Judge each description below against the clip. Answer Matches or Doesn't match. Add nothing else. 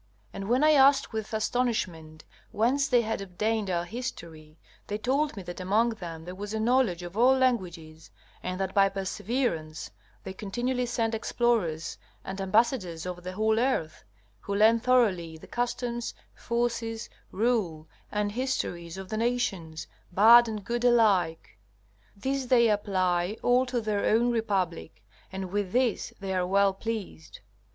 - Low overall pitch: Doesn't match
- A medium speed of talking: Matches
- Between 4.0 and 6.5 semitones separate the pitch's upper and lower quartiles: Matches